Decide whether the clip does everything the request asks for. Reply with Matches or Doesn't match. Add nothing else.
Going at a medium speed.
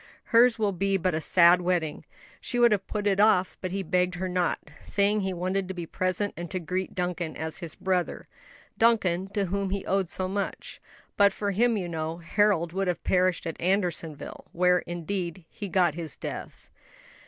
Matches